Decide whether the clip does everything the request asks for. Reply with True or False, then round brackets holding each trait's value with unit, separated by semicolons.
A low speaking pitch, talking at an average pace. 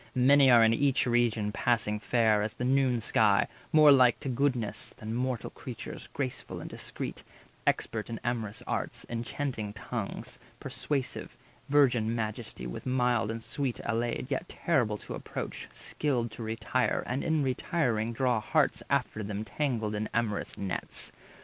True (120 Hz; 150 wpm)